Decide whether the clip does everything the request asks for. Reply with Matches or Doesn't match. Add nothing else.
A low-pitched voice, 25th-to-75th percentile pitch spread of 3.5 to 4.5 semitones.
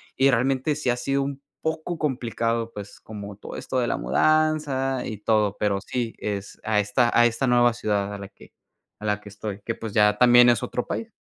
Matches